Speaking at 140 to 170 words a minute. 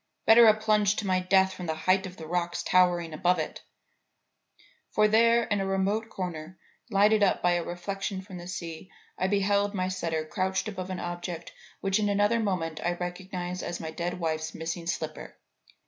No: average, 185 wpm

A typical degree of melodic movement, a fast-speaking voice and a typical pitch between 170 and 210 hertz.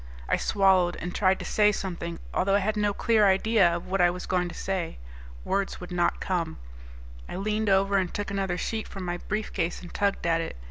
No: narrow, 2.3 semitones; fast, 215 wpm; high, 190 Hz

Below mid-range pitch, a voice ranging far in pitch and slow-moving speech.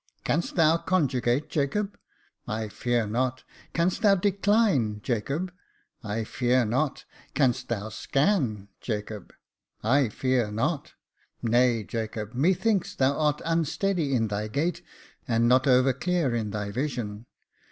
Yes: low, 130 Hz; wide, 6.3 semitones; slow, 130 wpm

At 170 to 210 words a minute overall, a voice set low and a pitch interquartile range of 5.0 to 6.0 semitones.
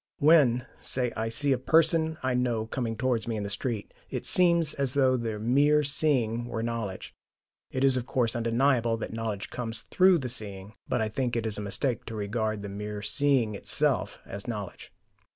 No: average, 190 wpm; low, 120 Hz; average, 3.5 semitones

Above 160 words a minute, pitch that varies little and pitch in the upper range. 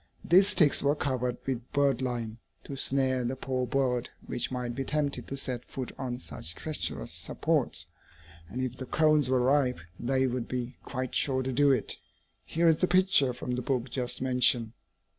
No: average, 180 wpm; narrow, 2.1 semitones; low, 130 Hz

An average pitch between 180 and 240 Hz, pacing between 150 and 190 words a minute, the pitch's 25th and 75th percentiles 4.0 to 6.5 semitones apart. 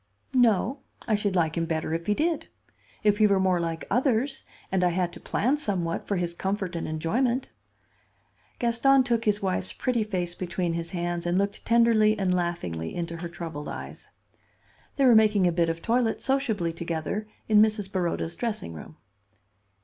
Yes: high, 190 Hz; average, 175 wpm; average, 4.7 semitones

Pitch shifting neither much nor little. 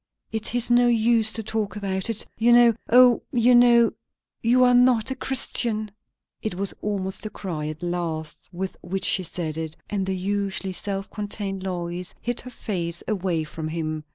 Yes: average, 4.7 semitones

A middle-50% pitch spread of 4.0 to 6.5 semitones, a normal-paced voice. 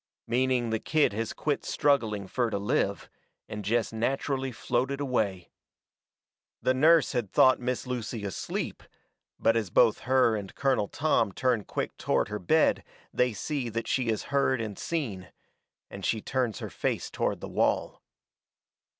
No: average, 3.6 semitones; average, 155 wpm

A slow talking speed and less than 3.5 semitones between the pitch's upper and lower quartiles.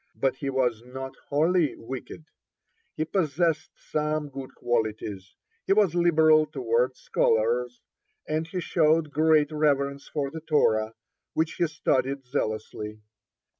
No: slow, 125 wpm; average, 4.2 semitones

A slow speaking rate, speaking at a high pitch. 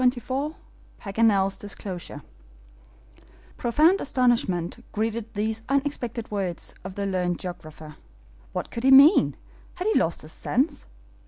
Yes: slow, 120 wpm; high, 220 Hz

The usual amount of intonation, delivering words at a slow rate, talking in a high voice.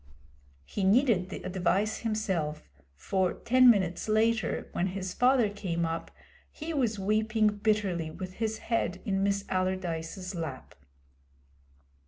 Yes: average, 3.1 semitones; slow, 125 wpm; high, 195 Hz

